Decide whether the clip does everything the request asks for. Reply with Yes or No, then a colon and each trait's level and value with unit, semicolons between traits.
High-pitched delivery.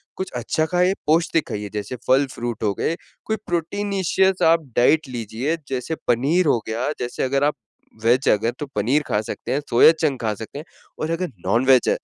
No: low, 135 Hz